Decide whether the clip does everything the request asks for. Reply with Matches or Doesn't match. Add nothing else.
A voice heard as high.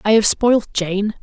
Matches